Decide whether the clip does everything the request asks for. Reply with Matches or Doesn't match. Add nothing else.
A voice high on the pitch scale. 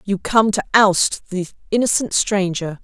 Matches